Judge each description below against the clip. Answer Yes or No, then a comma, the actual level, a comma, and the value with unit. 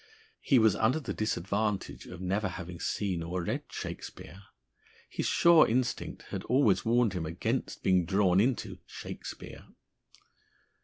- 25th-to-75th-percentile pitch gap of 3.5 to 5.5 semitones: Yes, average, 4.0 semitones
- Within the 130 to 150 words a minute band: Yes, slow, 135 wpm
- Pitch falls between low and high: No, low, 100 Hz